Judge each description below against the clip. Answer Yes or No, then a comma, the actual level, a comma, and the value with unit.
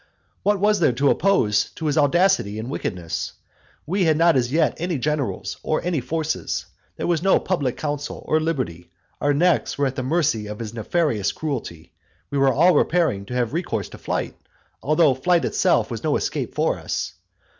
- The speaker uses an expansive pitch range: Yes, wide, 5.9 semitones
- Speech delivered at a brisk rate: No, average, 185 wpm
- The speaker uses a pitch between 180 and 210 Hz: No, medium, 145 Hz